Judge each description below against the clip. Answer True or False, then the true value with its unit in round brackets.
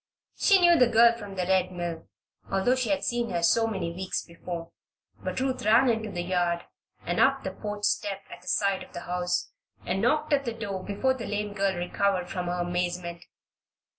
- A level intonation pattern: False (4.5 semitones)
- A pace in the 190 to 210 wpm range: True (200 wpm)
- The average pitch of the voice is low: False (195 Hz)